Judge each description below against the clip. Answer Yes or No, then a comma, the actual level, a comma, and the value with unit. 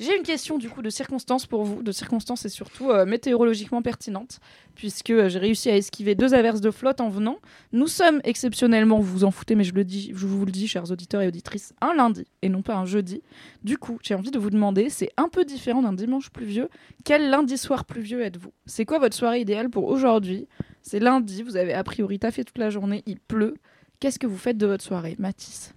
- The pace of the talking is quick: Yes, fast, 235 wpm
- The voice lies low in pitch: No, high, 225 Hz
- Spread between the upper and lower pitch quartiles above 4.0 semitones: No, average, 3.7 semitones